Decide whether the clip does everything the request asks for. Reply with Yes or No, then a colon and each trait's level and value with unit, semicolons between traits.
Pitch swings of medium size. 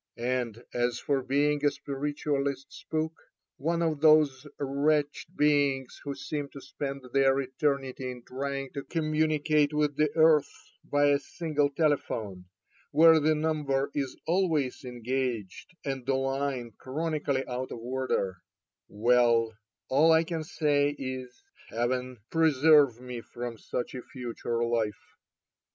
Yes: average, 3.0 semitones